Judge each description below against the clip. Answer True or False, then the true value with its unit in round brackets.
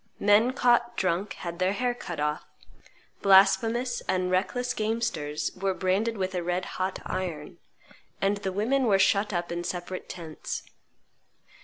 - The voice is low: False (190 Hz)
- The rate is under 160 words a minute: True (145 wpm)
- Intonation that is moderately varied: True (3.7 semitones)